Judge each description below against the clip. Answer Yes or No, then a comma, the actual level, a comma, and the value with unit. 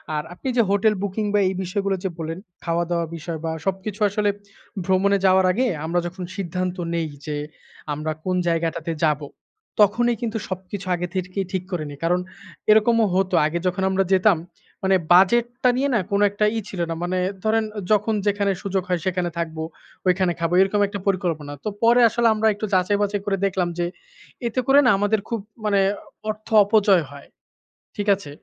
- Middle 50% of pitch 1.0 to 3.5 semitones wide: Yes, average, 3.0 semitones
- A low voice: No, high, 190 Hz